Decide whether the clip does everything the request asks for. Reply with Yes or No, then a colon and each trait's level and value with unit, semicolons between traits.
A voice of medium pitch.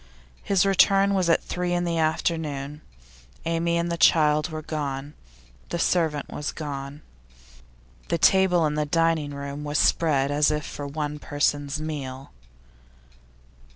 Yes: medium, 155 Hz